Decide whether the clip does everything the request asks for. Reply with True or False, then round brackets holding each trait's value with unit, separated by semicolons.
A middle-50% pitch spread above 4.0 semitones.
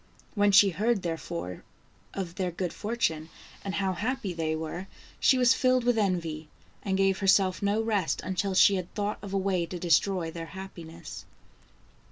False (3.3 semitones)